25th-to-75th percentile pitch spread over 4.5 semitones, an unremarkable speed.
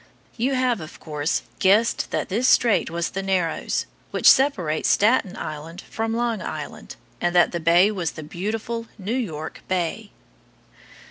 Yes: average, 5.3 semitones; average, 150 wpm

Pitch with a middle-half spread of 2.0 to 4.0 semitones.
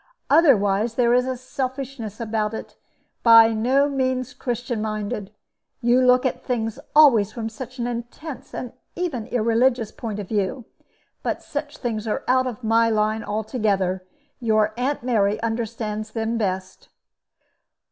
Yes: average, 2.8 semitones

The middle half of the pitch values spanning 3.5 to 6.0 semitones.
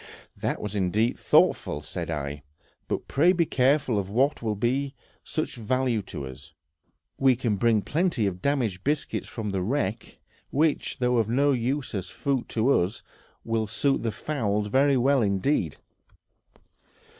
Yes: average, 5.2 semitones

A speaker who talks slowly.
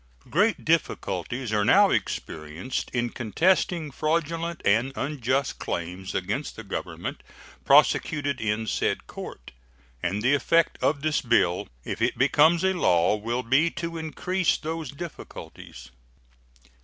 Yes: slow, 125 wpm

